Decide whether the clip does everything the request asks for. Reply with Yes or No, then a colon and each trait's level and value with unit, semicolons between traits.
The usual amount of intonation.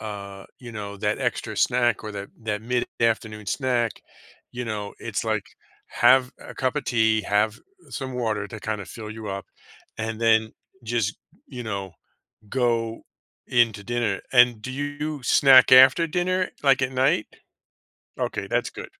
Yes: average, 3.3 semitones